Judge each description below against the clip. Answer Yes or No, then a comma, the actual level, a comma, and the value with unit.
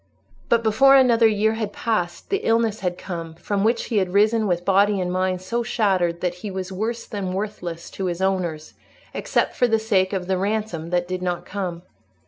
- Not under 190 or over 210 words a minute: Yes, average, 200 wpm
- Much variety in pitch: No, average, 3.5 semitones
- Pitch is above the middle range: Yes, high, 195 Hz